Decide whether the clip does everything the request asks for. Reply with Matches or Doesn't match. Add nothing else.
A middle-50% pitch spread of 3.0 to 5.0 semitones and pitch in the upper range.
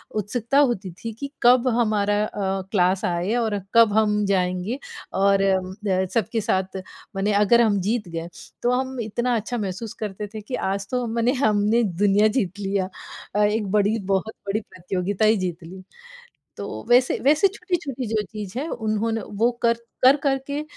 Matches